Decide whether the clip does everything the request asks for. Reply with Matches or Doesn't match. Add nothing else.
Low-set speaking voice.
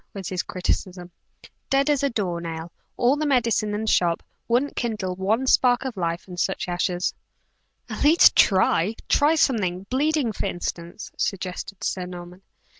Doesn't match